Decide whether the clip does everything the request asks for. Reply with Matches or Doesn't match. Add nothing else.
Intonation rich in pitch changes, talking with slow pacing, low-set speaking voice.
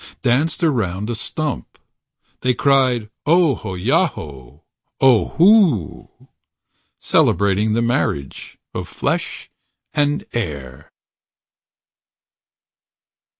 Matches